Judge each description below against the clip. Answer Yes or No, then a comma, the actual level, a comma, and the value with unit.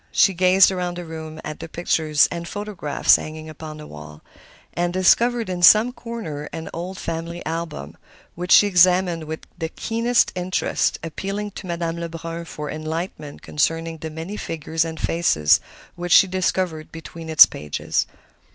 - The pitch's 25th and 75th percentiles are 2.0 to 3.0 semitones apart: Yes, average, 2.7 semitones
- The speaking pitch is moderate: Yes, medium, 165 Hz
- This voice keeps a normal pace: Yes, average, 155 wpm